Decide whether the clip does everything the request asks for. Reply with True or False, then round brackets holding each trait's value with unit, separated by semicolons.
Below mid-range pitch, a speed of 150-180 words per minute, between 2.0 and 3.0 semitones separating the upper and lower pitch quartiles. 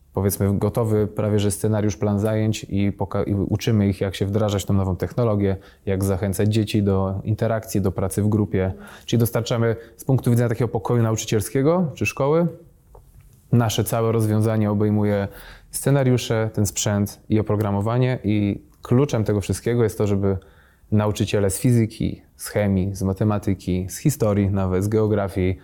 True (105 Hz; 155 wpm; 2.5 semitones)